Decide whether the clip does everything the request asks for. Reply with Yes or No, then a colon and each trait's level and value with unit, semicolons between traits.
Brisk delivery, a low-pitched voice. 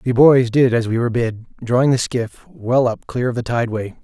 Yes: fast, 240 wpm; low, 120 Hz